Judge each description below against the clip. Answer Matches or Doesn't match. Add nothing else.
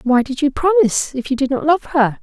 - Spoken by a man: Doesn't match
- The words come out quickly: Matches